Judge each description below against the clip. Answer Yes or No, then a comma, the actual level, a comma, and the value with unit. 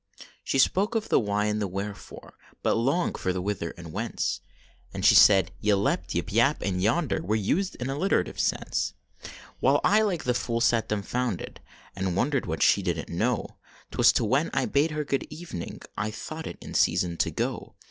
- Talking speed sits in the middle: Yes, average, 190 wpm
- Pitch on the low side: Yes, low, 110 Hz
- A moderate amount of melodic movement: No, wide, 6.5 semitones